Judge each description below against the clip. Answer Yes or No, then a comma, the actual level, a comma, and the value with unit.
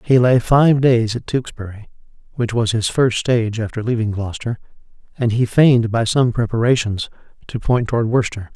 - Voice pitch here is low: Yes, low, 115 Hz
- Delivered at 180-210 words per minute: No, average, 170 wpm